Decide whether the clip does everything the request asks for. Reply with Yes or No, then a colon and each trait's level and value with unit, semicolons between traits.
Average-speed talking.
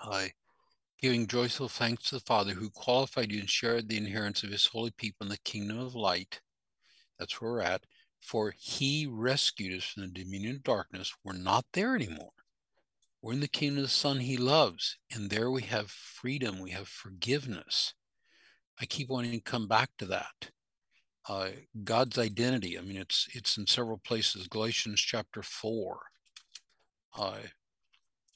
Yes: average, 170 wpm